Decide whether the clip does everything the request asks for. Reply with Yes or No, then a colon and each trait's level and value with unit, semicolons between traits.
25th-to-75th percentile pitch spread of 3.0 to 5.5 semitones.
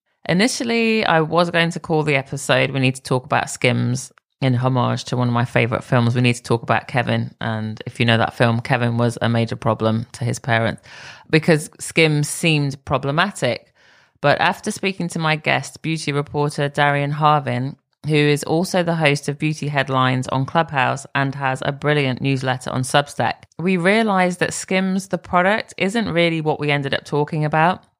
Yes: average, 4.4 semitones